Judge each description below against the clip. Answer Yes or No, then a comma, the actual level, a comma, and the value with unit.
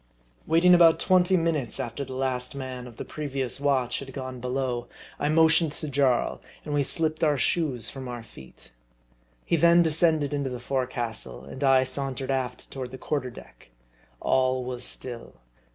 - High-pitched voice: No, low, 135 Hz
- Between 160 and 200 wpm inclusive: Yes, average, 170 wpm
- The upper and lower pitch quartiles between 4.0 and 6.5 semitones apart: No, average, 3.4 semitones